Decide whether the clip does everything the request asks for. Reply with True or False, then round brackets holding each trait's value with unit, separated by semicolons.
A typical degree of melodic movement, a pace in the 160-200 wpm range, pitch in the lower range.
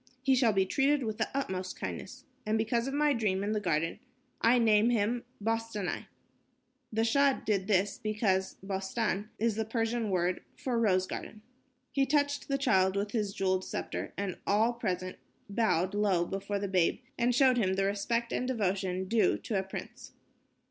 False (3.5 semitones; 175 wpm; 215 Hz)